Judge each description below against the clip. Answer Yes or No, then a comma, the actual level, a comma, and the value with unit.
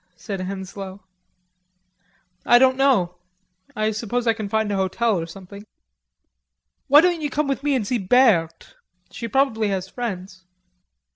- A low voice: No, high, 215 Hz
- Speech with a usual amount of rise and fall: Yes, average, 4.8 semitones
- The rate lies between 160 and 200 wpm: No, average, 145 wpm